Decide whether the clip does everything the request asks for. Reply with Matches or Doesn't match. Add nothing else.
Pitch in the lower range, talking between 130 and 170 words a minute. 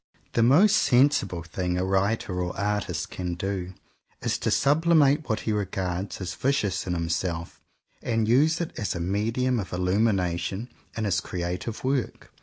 Matches